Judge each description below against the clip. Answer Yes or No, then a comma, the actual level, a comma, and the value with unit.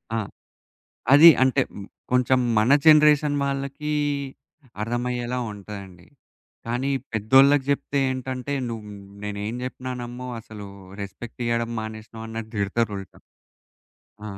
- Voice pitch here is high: No, low, 120 Hz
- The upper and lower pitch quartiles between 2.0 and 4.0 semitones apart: Yes, average, 3.4 semitones